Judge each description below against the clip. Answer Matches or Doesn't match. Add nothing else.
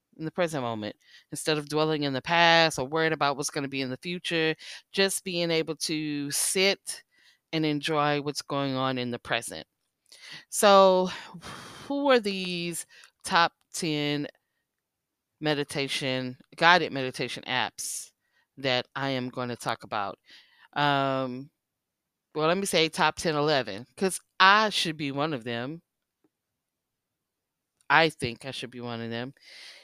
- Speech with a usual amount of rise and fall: Matches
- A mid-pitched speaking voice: Matches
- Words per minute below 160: Matches